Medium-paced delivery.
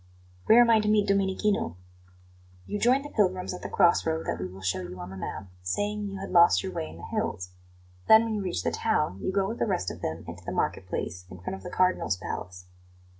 No: fast, 240 wpm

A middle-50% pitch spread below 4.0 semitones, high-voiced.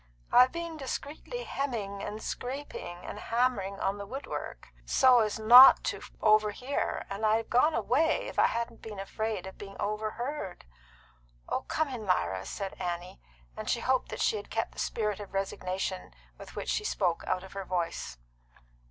No: average, 4.8 semitones; high, 215 Hz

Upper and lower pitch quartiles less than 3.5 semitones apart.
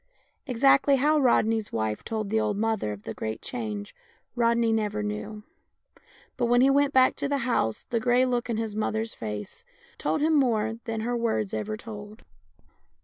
Yes: average, 2.7 semitones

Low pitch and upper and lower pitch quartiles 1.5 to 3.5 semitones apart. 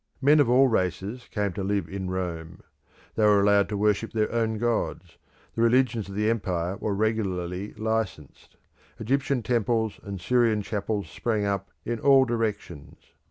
Yes: low, 105 Hz; average, 2.9 semitones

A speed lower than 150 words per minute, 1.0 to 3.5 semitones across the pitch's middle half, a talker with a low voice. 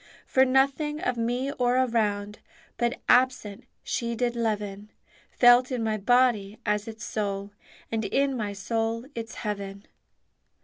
No: slow, 135 wpm; average, 3.2 semitones; high, 230 Hz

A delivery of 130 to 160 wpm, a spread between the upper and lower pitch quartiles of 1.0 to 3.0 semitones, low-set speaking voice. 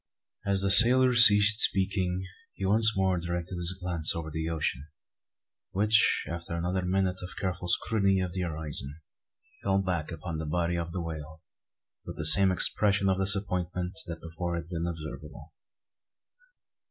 Yes: average, 155 wpm; narrow, 2.6 semitones; very low, 90 Hz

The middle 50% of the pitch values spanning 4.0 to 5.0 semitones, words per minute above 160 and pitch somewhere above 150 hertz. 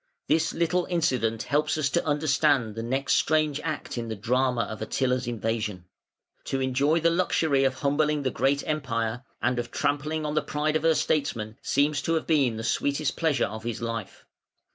No: average, 4.7 semitones; average, 185 wpm; medium, 140 Hz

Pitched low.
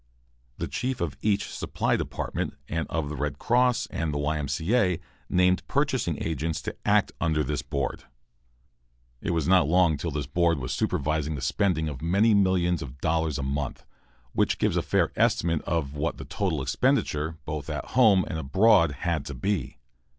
Yes: very low, 80 Hz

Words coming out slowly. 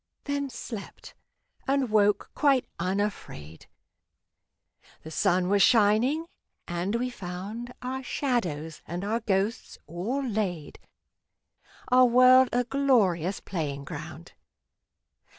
Yes: slow, 100 wpm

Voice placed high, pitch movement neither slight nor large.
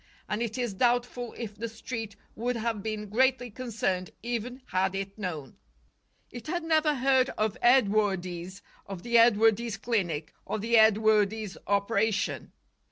Yes: high, 220 Hz; average, 3.3 semitones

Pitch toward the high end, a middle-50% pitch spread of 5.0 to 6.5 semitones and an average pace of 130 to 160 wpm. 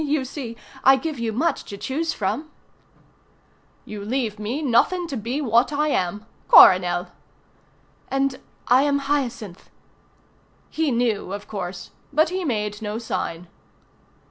Yes: high, 240 Hz; wide, 5.4 semitones; average, 140 wpm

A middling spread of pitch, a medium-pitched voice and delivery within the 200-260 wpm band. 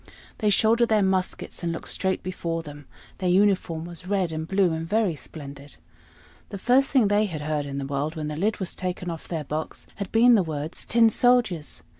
Yes: average, 4.7 semitones; medium, 180 Hz; fast, 205 wpm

